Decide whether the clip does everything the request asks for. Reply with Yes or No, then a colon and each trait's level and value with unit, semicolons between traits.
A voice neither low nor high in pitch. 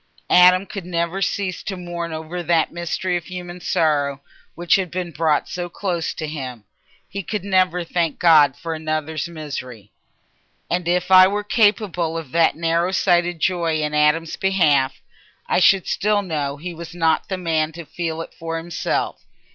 Yes: medium, 170 Hz